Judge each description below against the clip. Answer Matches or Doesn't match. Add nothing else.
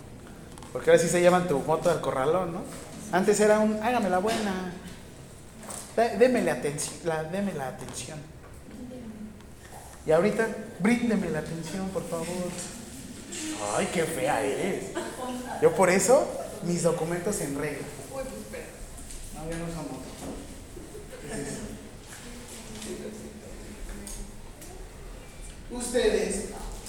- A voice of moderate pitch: Matches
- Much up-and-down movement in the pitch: Matches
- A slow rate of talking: Matches